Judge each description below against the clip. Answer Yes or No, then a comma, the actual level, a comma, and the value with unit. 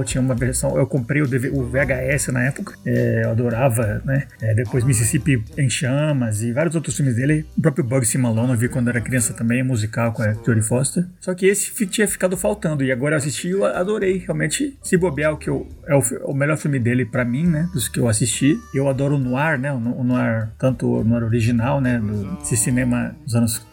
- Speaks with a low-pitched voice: Yes, low, 130 Hz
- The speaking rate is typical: No, fast, 225 wpm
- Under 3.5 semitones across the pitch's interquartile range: No, average, 3.8 semitones